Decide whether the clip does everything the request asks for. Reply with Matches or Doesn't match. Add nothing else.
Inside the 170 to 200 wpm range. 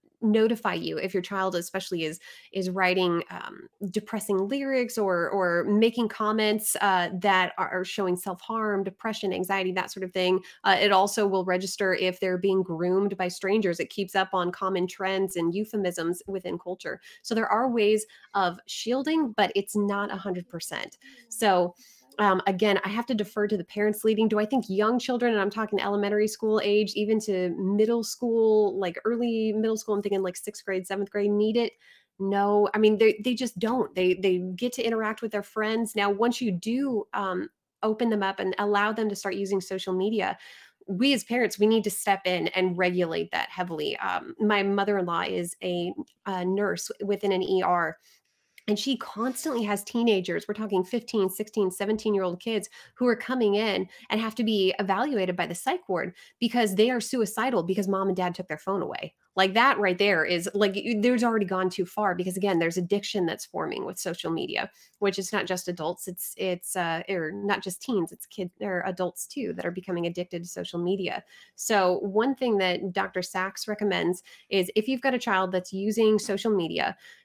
Matches